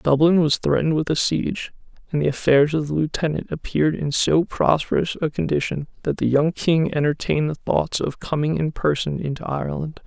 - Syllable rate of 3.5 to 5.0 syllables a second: No, 5.4 syllables/s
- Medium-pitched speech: Yes, medium, 150 Hz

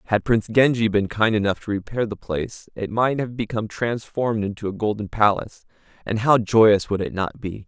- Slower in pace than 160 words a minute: No, fast, 205 wpm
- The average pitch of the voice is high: No, low, 105 Hz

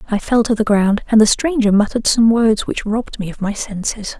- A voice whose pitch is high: Yes, high, 220 Hz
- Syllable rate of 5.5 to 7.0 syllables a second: Yes, 5.6 syllables/s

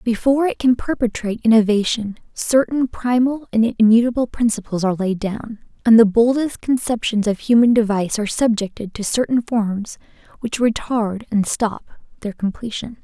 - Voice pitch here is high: Yes, high, 225 Hz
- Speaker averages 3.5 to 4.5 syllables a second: No, 5.2 syllables/s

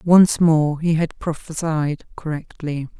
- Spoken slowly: Yes, slow, 120 wpm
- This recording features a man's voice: No, female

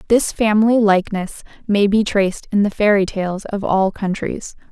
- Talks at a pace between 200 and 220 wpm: No, average, 165 wpm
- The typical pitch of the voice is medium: No, high, 205 Hz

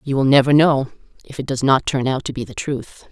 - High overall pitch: No, low, 135 Hz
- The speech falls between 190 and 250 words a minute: No, fast, 270 wpm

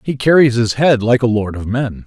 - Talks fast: Yes, fast, 260 wpm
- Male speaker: Yes, male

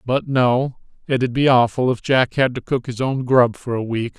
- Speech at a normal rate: No, fast, 215 wpm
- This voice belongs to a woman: No, male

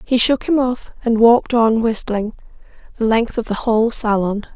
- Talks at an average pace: Yes, average, 185 wpm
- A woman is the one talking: Yes, female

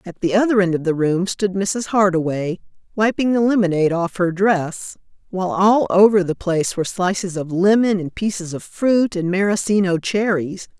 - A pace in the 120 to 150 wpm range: No, average, 180 wpm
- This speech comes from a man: No, female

